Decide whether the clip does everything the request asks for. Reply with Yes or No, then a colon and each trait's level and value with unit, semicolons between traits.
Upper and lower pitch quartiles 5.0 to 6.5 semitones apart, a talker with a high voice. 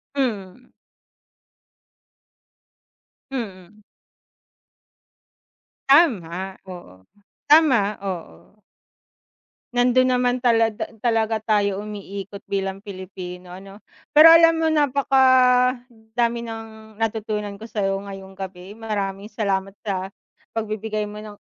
No: average, 3.8 semitones; high, 215 Hz